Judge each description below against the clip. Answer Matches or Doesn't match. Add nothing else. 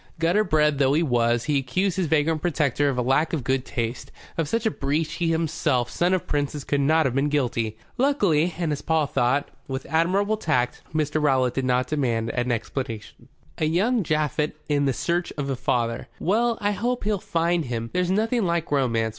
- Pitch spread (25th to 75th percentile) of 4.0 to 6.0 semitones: Matches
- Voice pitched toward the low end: Doesn't match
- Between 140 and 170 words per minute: Doesn't match